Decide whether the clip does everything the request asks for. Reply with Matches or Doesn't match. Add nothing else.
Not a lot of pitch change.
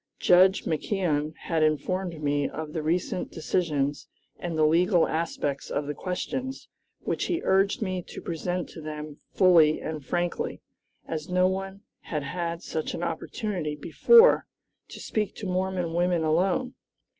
Doesn't match